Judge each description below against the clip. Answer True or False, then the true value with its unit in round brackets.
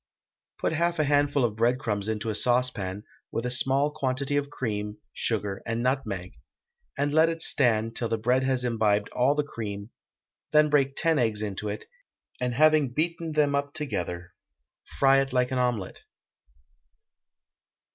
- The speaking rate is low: False (155 wpm)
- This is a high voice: False (125 Hz)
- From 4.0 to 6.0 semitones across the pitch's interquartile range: True (4.9 semitones)